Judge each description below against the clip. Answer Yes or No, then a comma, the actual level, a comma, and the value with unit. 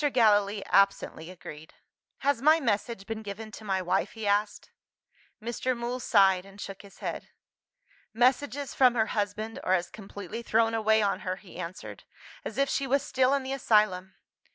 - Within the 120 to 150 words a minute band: No, average, 170 wpm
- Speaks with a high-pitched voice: Yes, high, 215 Hz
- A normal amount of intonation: Yes, average, 3.5 semitones